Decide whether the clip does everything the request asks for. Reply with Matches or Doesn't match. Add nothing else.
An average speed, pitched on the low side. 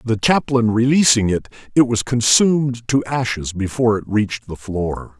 Matches